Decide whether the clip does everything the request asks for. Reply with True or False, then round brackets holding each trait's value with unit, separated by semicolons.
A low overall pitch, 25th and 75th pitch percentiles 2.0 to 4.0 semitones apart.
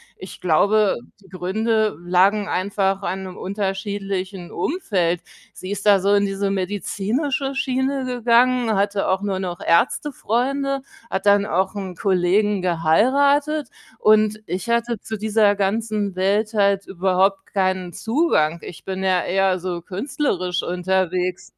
False (200 Hz; 2.9 semitones)